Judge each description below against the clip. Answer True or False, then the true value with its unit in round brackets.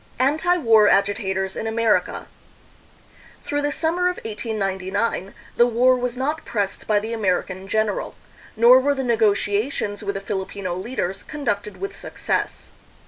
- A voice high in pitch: True (220 Hz)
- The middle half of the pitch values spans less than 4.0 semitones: False (4.3 semitones)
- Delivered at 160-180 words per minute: False (140 wpm)